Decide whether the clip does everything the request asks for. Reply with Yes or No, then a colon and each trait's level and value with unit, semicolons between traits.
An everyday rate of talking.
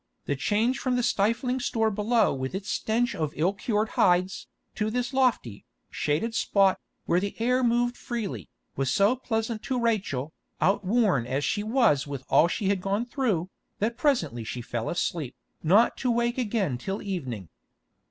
Yes: average, 165 wpm